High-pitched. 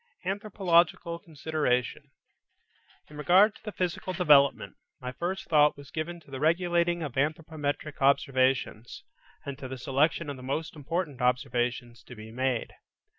No: medium, 150 Hz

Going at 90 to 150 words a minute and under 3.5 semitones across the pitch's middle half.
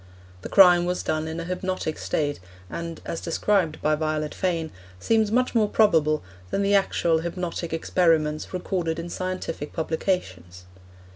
Yes: average, 145 wpm; average, 2.9 semitones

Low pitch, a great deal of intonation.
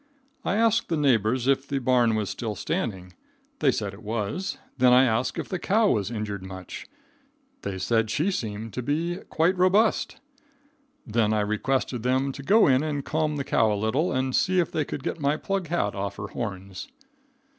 Yes: low, 125 Hz; wide, 6.4 semitones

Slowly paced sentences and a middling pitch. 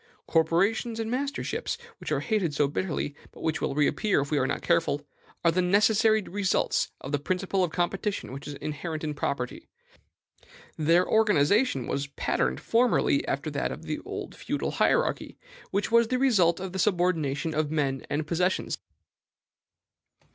No: average, 155 wpm; medium, 175 Hz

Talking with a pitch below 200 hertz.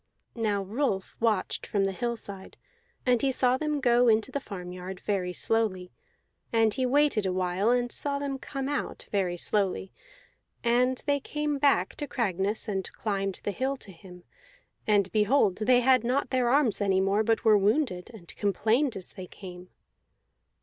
No: high, 220 Hz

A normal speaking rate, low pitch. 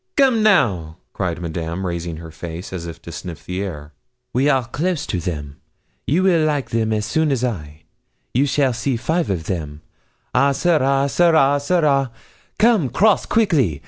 Yes: average, 175 wpm; low, 125 Hz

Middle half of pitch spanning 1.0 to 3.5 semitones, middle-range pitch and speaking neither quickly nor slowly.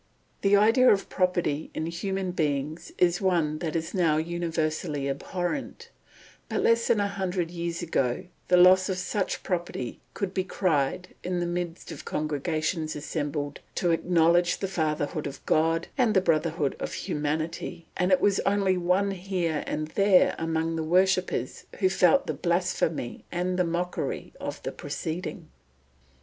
Yes: average, 2.9 semitones; medium, 175 Hz; average, 155 wpm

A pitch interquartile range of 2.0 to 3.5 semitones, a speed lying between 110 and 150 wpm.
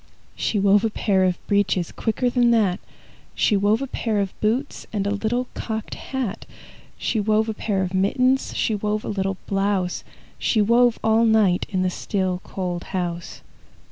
No: average, 2.8 semitones; average, 175 wpm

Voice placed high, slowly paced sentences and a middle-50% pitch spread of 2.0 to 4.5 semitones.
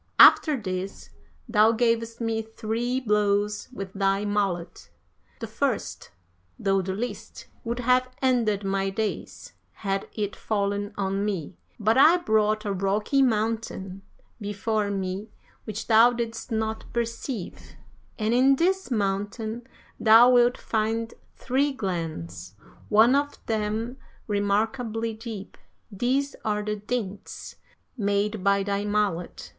Yes: high, 215 Hz; slow, 120 wpm; average, 2.7 semitones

